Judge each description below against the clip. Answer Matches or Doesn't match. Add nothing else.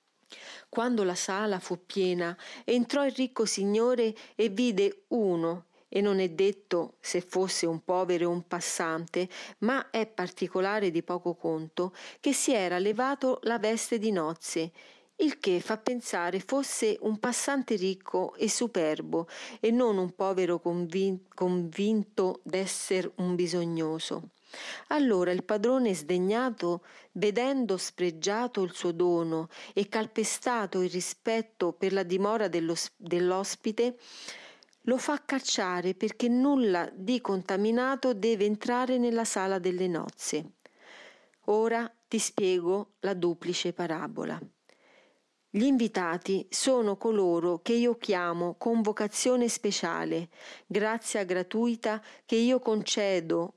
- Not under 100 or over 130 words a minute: Matches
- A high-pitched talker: Matches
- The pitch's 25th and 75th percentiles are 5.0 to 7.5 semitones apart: Doesn't match